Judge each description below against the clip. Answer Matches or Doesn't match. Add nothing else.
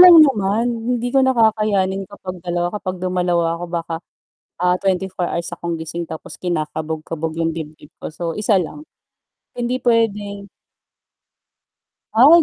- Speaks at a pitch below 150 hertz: Doesn't match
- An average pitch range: Matches